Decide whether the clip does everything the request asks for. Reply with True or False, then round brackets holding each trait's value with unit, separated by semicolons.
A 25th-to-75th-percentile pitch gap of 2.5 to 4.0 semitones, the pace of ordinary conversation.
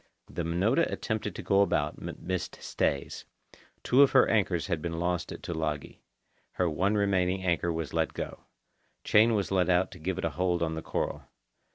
True (3.1 semitones; 190 wpm)